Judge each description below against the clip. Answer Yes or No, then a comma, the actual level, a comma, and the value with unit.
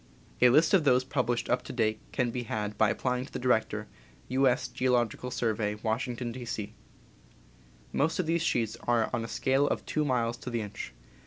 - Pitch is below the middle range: Yes, low, 125 Hz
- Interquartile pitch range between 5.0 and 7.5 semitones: No, narrow, 2.4 semitones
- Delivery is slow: No, average, 195 wpm